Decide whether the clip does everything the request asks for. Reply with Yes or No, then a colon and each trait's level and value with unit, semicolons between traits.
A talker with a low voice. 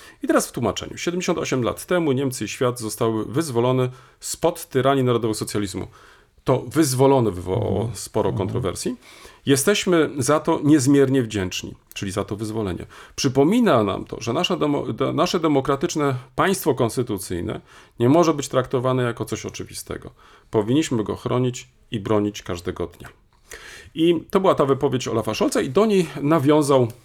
Yes: low, 130 Hz